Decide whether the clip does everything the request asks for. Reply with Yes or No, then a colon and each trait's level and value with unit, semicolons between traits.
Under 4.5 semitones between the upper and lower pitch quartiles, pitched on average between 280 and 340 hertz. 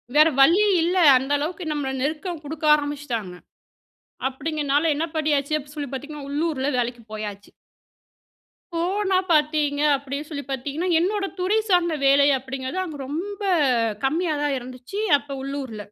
Yes: average, 3.3 semitones; very high, 290 Hz